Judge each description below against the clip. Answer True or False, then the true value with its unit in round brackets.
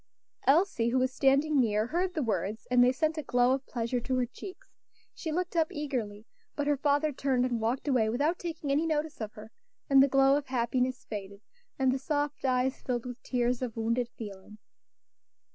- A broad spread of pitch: False (3.5 semitones)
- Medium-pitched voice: False (260 Hz)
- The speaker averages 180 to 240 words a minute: True (195 wpm)